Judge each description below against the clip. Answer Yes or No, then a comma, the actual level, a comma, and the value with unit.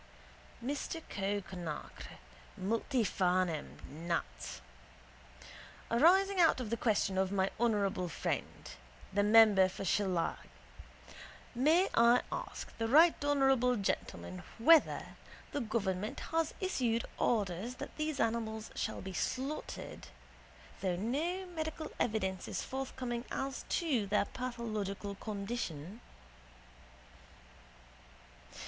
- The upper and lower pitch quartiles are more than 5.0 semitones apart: Yes, wide, 5.6 semitones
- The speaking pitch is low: No, high, 225 Hz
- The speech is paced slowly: Yes, slow, 100 wpm